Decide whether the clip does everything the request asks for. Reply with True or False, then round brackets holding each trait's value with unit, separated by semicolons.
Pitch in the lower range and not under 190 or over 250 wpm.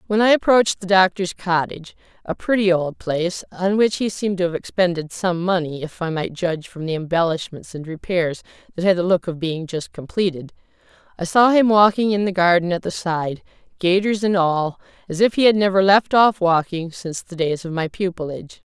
False (180 Hz; 195 wpm)